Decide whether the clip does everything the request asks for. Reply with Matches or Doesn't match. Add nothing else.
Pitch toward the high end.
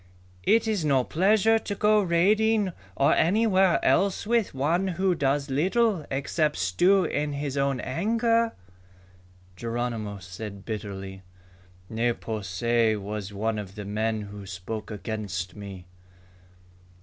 Doesn't match